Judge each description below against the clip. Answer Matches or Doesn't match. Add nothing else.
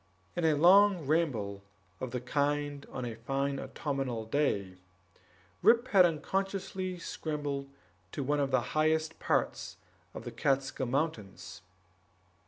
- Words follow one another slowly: Matches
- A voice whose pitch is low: Doesn't match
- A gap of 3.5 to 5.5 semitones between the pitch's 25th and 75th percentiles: Matches